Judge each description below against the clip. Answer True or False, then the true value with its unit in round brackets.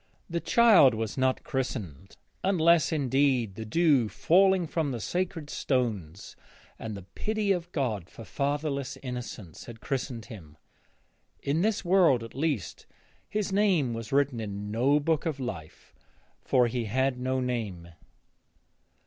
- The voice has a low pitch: True (130 Hz)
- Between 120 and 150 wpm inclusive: True (140 wpm)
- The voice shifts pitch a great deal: True (6.3 semitones)